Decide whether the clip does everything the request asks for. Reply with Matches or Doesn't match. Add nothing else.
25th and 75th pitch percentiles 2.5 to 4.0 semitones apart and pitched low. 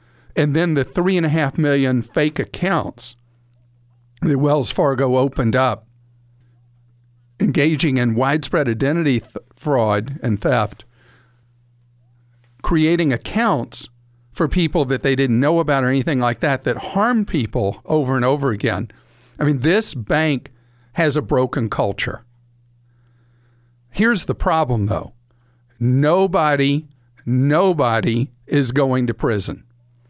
Matches